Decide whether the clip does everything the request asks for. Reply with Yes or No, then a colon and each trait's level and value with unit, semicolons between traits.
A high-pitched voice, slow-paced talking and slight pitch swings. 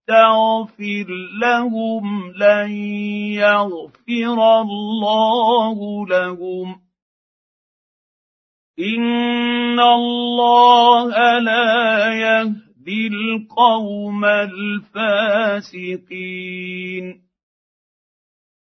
Yes: high, 215 Hz; slow, 40 wpm; narrow, 2.1 semitones